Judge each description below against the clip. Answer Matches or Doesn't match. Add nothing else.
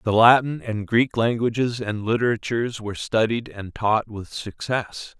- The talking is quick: Doesn't match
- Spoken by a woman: Doesn't match